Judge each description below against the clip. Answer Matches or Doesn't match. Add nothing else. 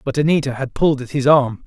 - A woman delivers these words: Doesn't match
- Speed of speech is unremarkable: Doesn't match